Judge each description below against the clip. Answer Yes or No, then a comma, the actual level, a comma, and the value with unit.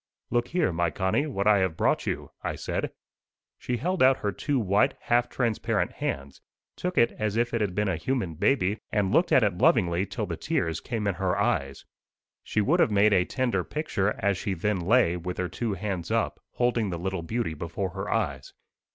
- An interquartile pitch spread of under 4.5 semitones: No, average, 4.8 semitones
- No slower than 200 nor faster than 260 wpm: Yes, fast, 205 wpm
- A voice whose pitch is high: No, low, 100 Hz